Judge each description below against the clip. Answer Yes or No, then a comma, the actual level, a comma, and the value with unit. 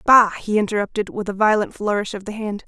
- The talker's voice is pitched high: Yes, high, 210 Hz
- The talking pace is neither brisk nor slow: No, fast, 225 wpm